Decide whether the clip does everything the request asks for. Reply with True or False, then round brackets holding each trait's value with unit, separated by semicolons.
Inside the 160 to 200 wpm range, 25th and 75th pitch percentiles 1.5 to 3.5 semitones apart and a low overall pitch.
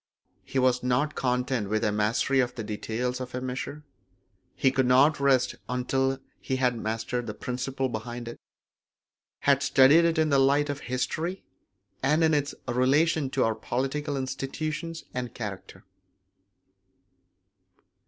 False (145 wpm; 2.5 semitones; 130 Hz)